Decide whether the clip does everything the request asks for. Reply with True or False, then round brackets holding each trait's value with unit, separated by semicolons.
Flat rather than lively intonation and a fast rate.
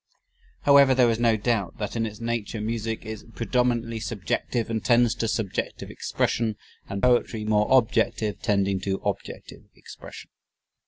False (2.0 semitones; 145 wpm)